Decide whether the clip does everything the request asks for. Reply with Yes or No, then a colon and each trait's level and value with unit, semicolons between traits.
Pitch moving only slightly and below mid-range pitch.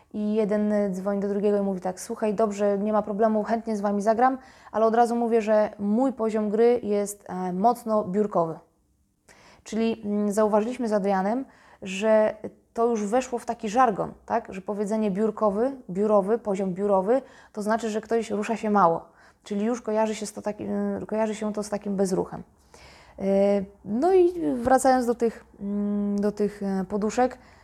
No: narrow, 2.1 semitones; high, 215 Hz